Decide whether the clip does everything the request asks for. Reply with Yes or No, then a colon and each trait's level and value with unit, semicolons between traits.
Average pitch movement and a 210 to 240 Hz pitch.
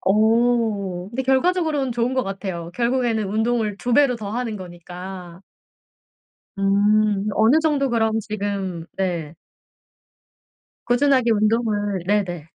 Yes: average, 3.9 semitones; high, 215 Hz